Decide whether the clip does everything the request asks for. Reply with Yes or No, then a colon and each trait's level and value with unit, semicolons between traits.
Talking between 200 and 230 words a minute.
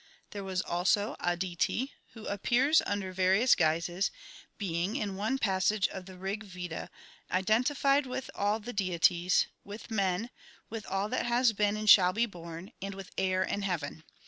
No: average, 160 wpm